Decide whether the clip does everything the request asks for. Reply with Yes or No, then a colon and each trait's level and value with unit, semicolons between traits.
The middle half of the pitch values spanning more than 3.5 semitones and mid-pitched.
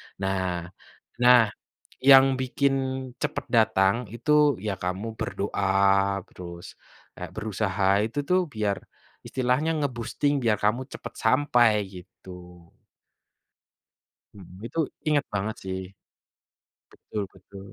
No: average, 5.0 semitones; low, 105 Hz